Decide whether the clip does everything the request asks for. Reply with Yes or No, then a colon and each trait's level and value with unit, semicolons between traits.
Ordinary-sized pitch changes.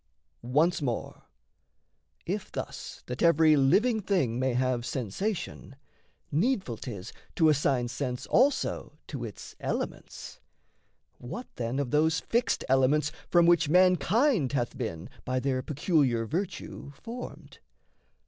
No: wide, 5.7 semitones